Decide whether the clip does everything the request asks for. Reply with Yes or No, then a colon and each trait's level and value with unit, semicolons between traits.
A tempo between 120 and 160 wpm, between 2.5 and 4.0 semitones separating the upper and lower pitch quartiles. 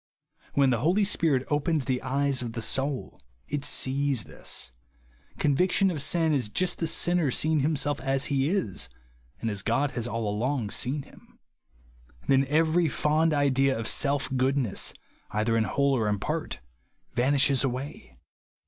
Yes: average, 155 wpm; average, 3.3 semitones